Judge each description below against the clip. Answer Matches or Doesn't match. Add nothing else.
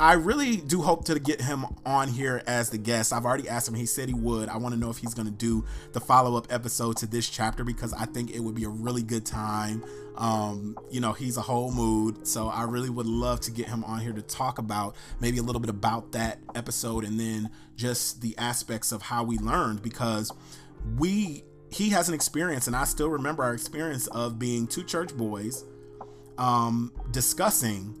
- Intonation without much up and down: Matches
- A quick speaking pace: Matches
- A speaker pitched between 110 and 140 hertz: Matches